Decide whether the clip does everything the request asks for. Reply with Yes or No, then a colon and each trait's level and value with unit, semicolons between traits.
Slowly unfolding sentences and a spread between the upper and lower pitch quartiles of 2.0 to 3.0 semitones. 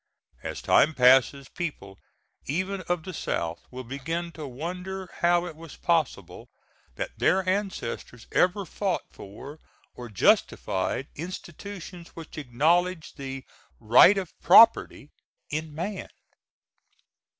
No: slow, 115 wpm; wide, 5.5 semitones